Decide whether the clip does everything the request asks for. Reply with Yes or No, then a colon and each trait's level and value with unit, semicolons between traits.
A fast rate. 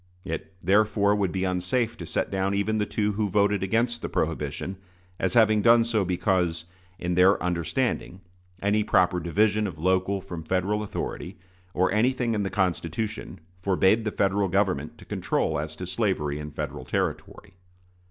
No: average, 160 wpm